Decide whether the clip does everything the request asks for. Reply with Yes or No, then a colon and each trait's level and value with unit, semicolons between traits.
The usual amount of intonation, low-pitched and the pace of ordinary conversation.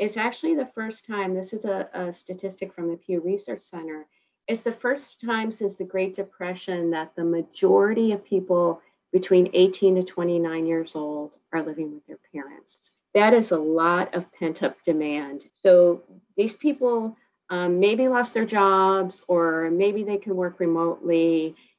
No: average, 3.6 semitones; medium, 185 Hz; average, 170 wpm